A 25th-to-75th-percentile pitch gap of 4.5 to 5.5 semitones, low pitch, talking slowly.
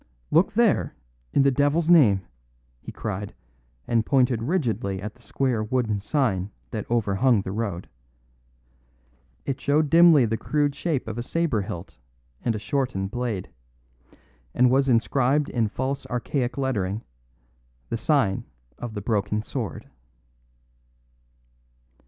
Yes: average, 4.8 semitones; low, 120 Hz; slow, 130 wpm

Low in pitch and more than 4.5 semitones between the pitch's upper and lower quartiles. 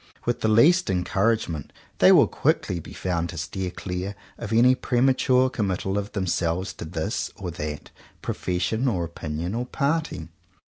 Yes: very low, 95 Hz; wide, 5.5 semitones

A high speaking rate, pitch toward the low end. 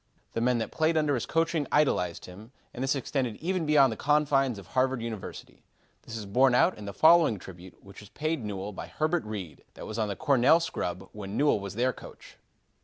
Yes: fast, 210 wpm; low, 125 Hz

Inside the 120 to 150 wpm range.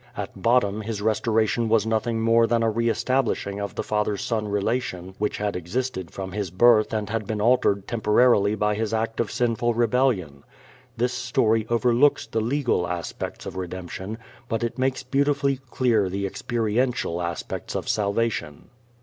No: average, 160 wpm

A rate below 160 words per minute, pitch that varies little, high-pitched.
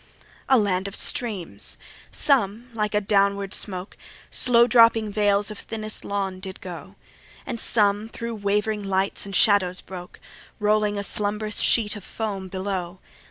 Yes: average, 145 wpm; narrow, 1.9 semitones; high, 205 Hz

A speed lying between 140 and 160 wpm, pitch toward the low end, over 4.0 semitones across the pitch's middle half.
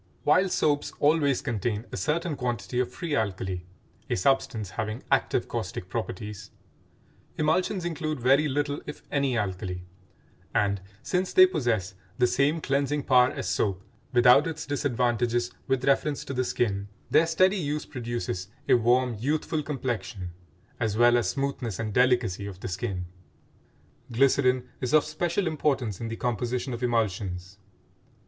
Yes: average, 145 wpm; low, 125 Hz; average, 5.1 semitones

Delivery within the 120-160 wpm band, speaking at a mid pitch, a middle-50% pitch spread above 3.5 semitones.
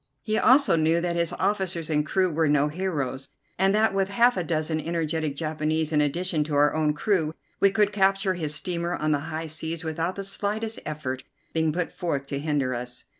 No: average, 200 wpm; medium, 160 Hz; average, 3.9 semitones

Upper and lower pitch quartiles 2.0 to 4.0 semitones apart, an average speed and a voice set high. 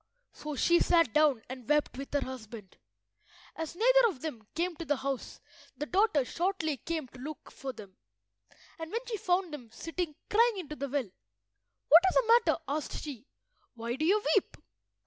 No: average, 5.3 semitones; average, 180 wpm; very high, 305 Hz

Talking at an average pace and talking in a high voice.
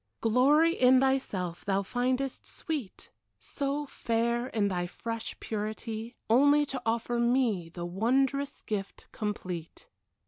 No: slow, 115 wpm; high, 235 Hz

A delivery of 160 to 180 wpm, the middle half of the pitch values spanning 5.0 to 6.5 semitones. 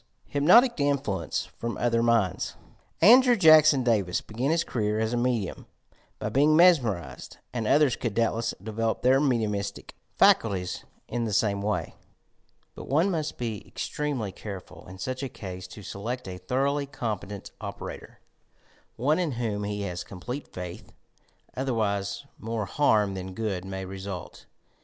No: average, 145 wpm; wide, 5.5 semitones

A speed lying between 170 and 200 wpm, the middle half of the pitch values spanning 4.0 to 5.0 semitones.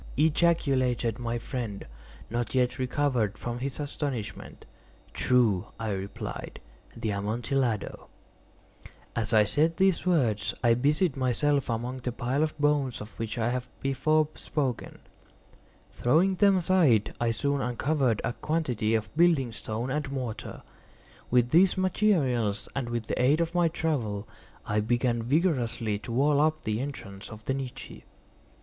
No: average, 140 wpm; average, 4.6 semitones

